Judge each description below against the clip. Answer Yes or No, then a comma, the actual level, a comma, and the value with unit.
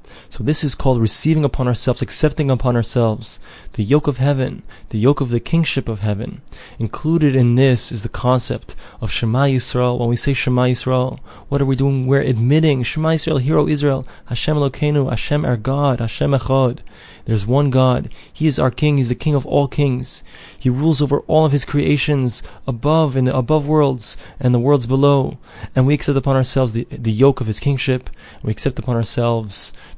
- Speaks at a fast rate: No, average, 190 wpm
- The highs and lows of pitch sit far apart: No, average, 3.1 semitones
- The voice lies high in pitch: No, low, 130 Hz